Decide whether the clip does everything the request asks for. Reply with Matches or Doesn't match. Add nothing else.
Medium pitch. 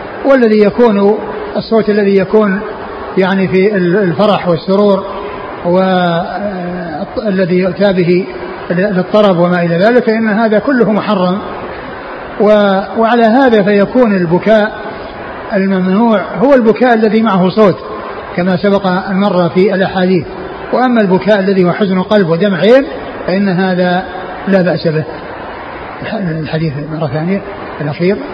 Doesn't match